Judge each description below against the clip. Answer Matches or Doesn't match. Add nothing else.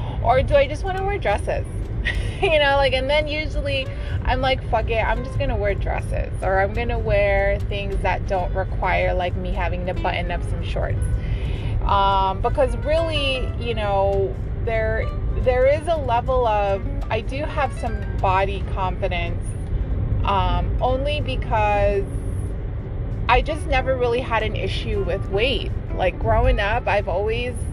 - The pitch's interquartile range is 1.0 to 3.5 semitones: Matches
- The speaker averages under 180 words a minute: Matches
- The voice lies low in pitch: Matches